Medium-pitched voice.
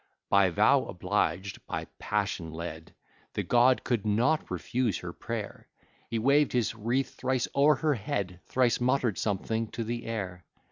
No: low, 115 Hz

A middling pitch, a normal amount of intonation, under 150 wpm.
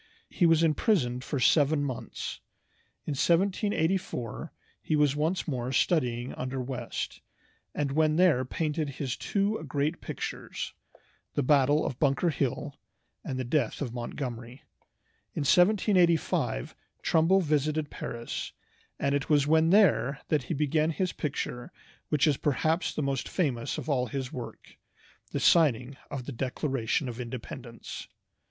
Yes: medium, 145 Hz; average, 3.9 semitones; slow, 135 wpm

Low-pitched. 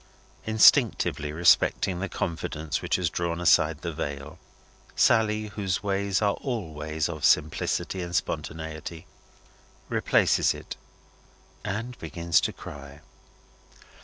Yes: very low, 85 Hz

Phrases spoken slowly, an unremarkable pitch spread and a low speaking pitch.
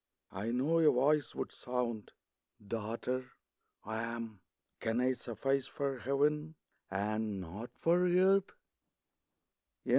Yes: slow, 115 wpm; average, 4.7 semitones; low, 125 Hz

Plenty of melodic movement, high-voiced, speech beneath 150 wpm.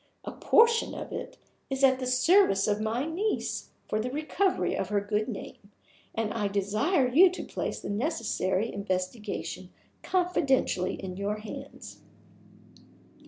Yes: wide, 7.1 semitones; high, 225 Hz; slow, 135 wpm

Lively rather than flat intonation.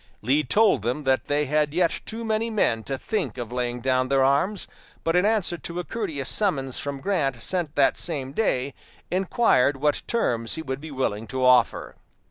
Yes: wide, 5.7 semitones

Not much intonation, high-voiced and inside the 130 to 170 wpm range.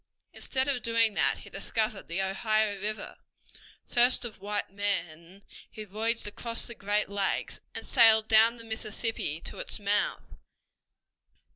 Yes: narrow, 2.1 semitones; high, 215 Hz; average, 140 wpm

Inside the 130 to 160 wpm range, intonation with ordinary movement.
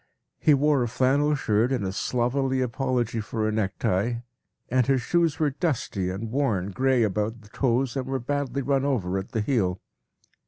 No: average, 180 wpm; average, 4.1 semitones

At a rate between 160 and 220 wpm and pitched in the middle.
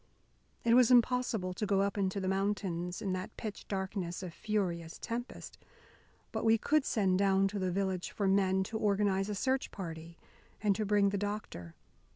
No: average, 180 wpm; high, 195 Hz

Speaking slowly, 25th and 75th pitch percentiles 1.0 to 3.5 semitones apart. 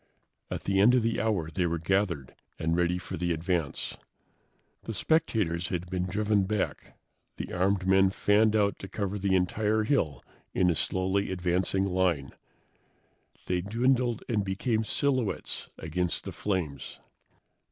No: average, 145 wpm; average, 3.2 semitones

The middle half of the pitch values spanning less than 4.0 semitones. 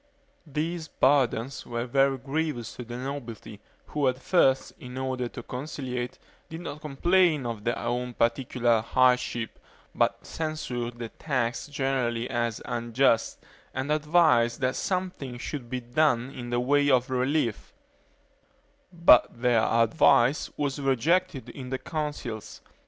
Yes: average, 3.5 semitones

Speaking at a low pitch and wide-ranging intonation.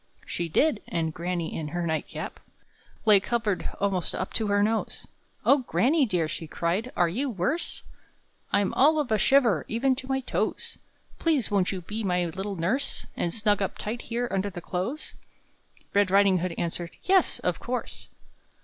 No: high, 200 Hz; wide, 5.7 semitones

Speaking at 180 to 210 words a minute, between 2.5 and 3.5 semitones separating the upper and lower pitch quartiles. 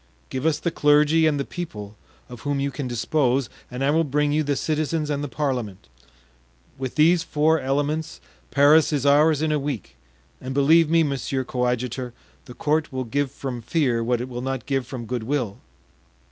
Yes: average, 190 wpm; average, 3.2 semitones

